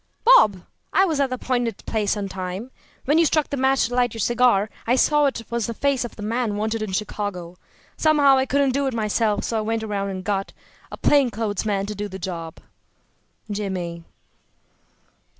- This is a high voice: Yes, high, 225 Hz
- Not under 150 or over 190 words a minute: No, average, 200 wpm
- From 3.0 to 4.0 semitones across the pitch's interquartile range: No, average, 4.6 semitones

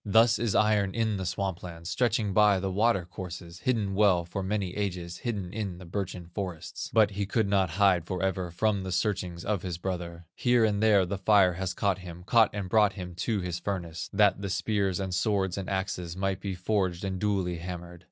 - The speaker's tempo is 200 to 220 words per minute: Yes, fast, 205 wpm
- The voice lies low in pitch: Yes, very low, 95 Hz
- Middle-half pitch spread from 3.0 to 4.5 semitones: No, narrow, 2.5 semitones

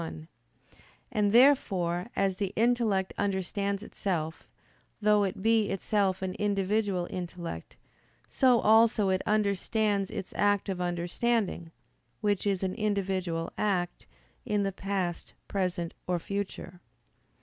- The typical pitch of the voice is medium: No, high, 195 Hz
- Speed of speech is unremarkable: No, slow, 115 wpm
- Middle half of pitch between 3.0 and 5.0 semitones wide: No, narrow, 2.5 semitones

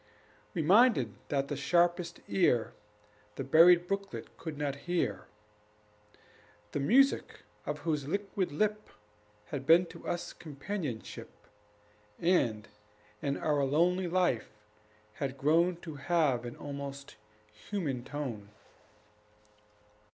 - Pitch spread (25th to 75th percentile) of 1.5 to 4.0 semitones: No, average, 4.4 semitones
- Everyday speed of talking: No, slow, 105 wpm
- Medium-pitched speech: Yes, medium, 150 Hz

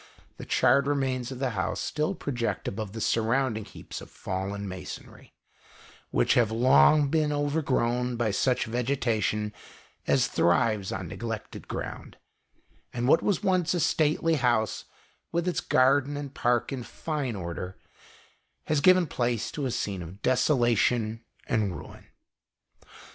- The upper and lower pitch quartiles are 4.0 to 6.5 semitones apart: Yes, average, 4.7 semitones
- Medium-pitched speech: No, low, 125 Hz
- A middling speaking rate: Yes, average, 145 wpm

